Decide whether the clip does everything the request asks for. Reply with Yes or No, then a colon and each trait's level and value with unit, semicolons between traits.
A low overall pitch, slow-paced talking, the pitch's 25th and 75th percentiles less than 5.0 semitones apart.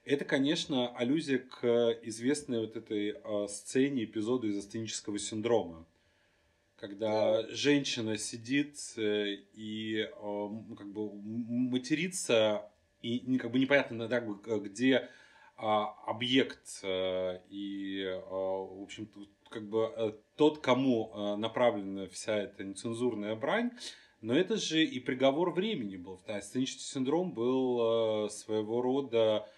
Yes: low, 110 Hz; slow, 100 wpm; average, 3.6 semitones